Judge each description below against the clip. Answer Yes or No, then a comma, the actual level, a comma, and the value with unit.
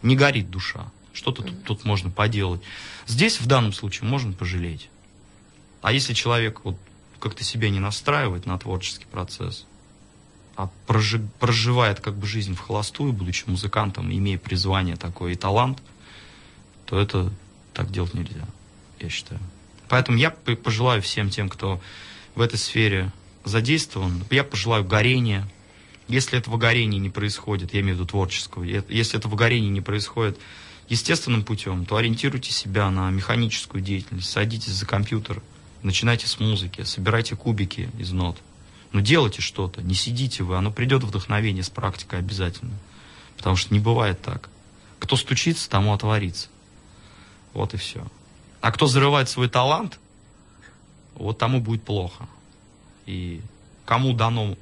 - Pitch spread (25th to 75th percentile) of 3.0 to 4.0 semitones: Yes, average, 3.3 semitones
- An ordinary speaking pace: Yes, average, 140 wpm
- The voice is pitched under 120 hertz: Yes, low, 105 Hz